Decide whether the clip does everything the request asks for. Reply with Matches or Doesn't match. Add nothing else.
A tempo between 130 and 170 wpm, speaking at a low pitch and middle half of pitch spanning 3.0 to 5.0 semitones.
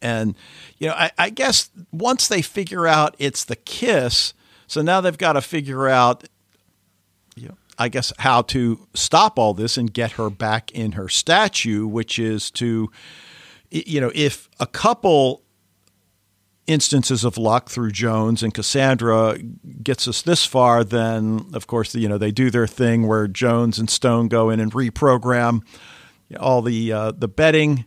Matches